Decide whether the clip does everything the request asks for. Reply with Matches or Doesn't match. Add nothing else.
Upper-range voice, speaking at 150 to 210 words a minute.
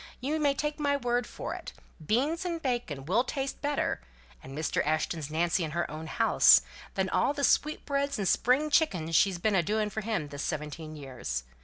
Matches